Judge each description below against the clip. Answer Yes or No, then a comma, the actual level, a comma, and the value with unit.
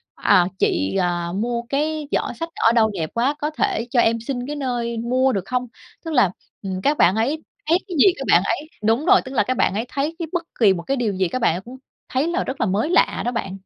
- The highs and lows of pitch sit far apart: Yes, wide, 6.0 semitones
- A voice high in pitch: Yes, high, 245 Hz